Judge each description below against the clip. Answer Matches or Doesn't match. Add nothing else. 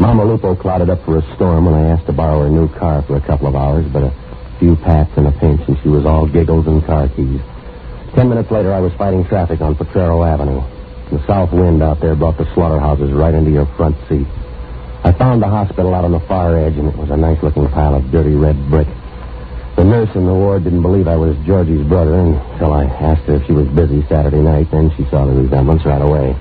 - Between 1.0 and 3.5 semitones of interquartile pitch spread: Matches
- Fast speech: Matches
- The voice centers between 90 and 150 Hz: Doesn't match